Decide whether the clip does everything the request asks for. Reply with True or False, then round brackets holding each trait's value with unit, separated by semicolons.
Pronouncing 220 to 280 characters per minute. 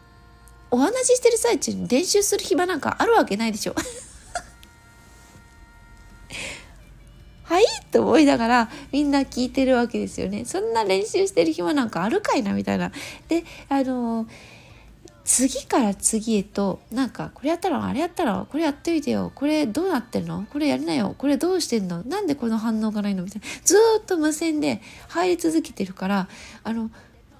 False (345 characters per minute)